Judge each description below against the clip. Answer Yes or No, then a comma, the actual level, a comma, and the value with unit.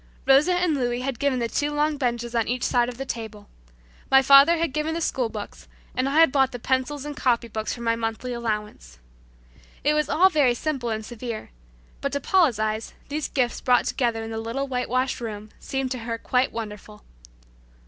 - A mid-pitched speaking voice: No, very high, 250 Hz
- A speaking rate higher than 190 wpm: Yes, average, 200 wpm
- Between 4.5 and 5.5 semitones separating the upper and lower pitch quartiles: No, average, 3.5 semitones